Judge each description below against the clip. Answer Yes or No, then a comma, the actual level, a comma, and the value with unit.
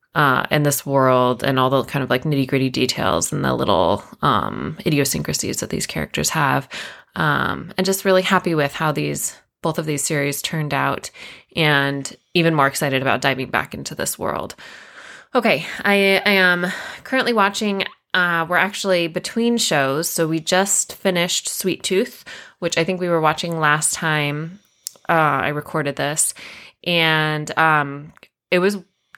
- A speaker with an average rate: Yes, average, 160 wpm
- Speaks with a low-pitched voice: No, medium, 160 Hz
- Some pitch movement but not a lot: Yes, average, 4.3 semitones